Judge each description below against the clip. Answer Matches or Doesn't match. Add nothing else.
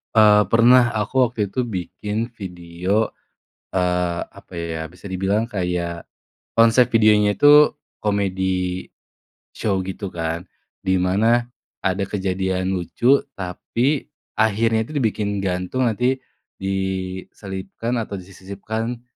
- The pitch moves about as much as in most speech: Matches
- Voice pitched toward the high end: Doesn't match